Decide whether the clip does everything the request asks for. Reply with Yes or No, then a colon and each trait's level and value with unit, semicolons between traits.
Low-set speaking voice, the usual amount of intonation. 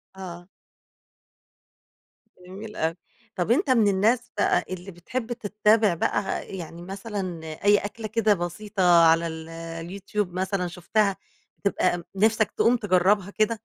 No: high, 195 Hz; average, 3.5 semitones